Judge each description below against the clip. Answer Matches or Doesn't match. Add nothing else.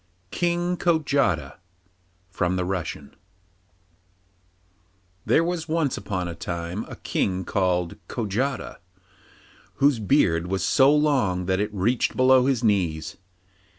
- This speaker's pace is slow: Matches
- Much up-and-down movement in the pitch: Matches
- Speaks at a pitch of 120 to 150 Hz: Doesn't match